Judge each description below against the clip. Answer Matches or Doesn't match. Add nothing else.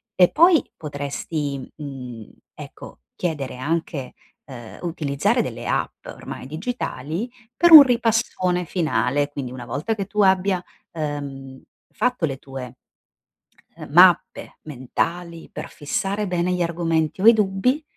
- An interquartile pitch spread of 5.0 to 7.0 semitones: Matches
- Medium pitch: Matches